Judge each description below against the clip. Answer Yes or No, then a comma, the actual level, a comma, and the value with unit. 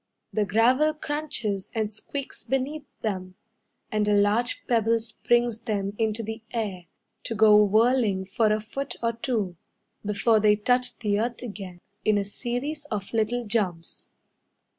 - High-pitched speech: Yes, high, 220 Hz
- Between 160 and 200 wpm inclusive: No, average, 145 wpm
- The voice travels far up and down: No, average, 2.8 semitones